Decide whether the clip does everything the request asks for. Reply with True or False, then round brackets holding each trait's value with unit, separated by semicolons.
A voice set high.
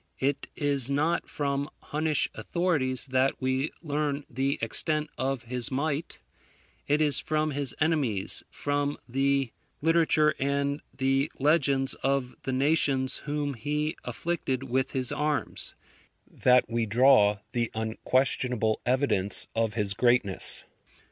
False (135 Hz)